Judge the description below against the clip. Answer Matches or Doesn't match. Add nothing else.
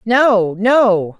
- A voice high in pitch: Matches